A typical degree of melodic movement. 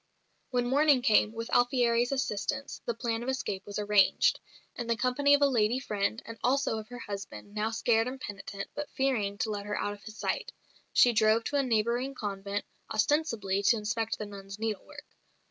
Yes: average, 3.3 semitones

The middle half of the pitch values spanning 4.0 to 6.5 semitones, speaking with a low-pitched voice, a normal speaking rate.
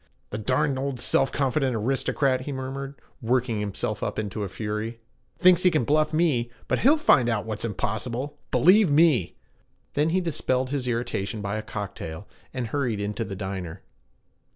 Yes: average, 5.0 semitones; low, 125 Hz; average, 165 wpm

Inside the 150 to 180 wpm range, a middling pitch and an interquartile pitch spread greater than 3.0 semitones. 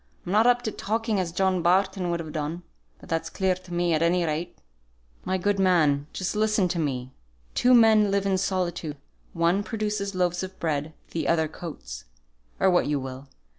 No: average, 190 wpm; medium, 180 Hz; average, 3.5 semitones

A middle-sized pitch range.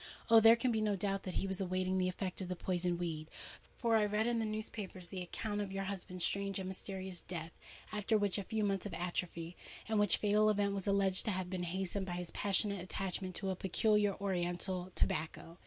No: narrow, 2.3 semitones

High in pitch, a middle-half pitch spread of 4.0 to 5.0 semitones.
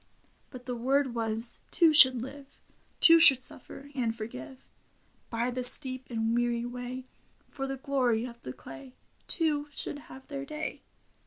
No: very high, 255 Hz; average, 2.8 semitones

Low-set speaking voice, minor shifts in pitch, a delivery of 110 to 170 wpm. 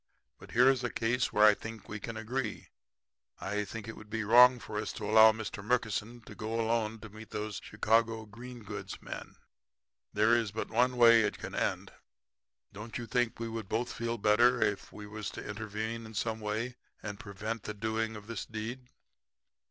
No: low, 110 Hz; narrow, 1.6 semitones; average, 200 wpm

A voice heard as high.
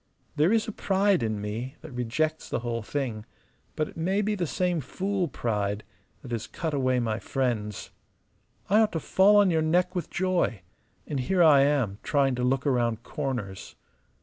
No: medium, 140 Hz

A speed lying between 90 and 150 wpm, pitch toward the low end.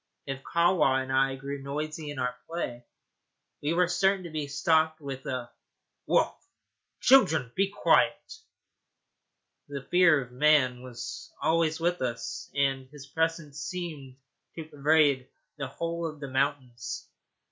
No: slow, 135 wpm; medium, 145 Hz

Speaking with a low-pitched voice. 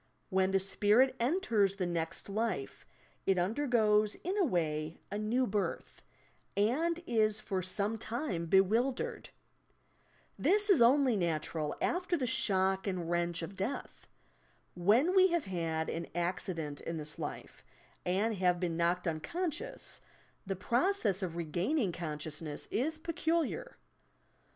No: high, 195 Hz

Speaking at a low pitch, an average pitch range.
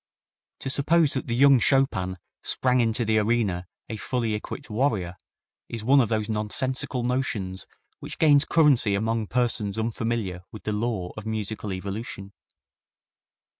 Yes: low, 110 Hz; average, 3.5 semitones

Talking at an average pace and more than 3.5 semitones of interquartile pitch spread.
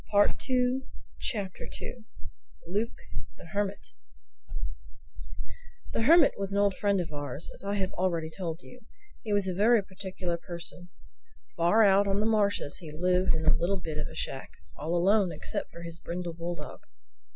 No: average, 160 wpm; average, 3.2 semitones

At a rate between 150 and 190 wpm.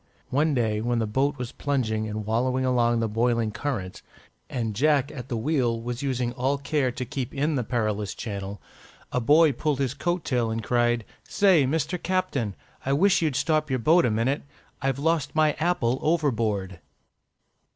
Yes: average, 175 wpm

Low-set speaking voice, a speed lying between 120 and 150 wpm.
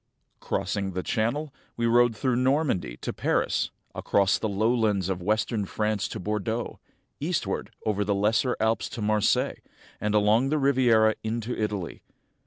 Yes: low, 110 Hz; average, 145 wpm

